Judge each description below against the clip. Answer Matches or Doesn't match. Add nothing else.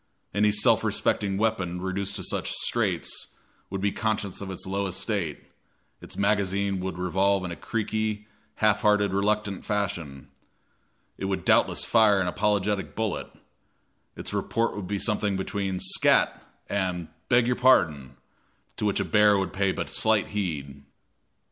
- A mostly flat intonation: Matches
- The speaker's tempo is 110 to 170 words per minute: Matches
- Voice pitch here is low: Matches